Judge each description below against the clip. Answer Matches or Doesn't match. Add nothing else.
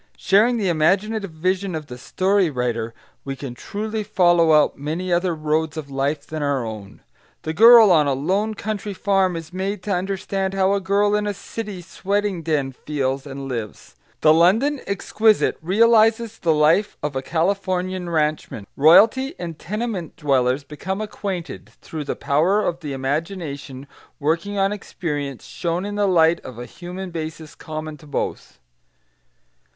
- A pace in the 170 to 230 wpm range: Doesn't match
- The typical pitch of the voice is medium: Matches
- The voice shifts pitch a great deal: Doesn't match